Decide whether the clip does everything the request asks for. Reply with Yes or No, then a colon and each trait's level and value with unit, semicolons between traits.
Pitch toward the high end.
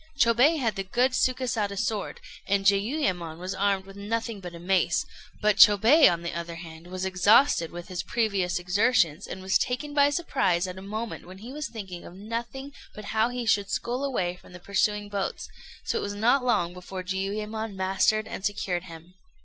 Yes: high, 200 Hz